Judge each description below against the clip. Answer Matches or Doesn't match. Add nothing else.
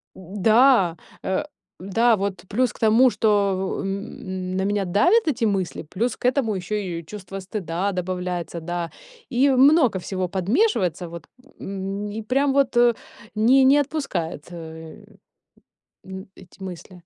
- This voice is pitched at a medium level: Doesn't match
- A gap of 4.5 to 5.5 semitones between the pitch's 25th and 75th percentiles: Matches